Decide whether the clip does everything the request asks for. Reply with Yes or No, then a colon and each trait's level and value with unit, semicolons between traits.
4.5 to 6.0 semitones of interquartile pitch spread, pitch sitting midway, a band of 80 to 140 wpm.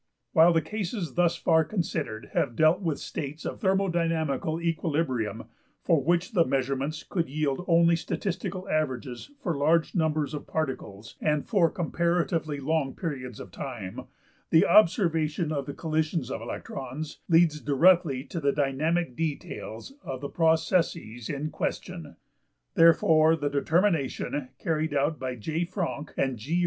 No: average, 3.4 semitones; medium, 155 Hz; slow, 135 wpm